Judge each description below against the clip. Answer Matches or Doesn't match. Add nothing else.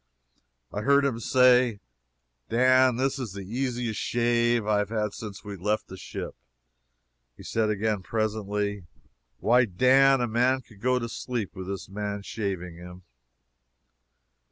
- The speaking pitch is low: Matches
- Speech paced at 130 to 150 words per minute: Matches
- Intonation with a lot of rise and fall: Doesn't match